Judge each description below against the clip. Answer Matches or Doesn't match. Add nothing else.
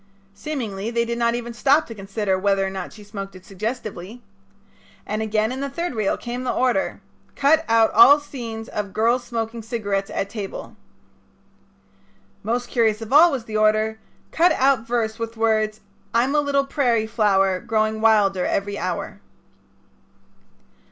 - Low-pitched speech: Doesn't match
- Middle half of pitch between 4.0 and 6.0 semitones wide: Doesn't match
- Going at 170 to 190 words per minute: Doesn't match